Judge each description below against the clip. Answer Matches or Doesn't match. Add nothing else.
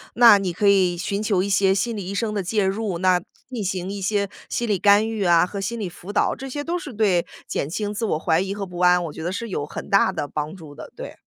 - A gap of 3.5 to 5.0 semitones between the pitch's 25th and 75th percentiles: Doesn't match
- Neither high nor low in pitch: Doesn't match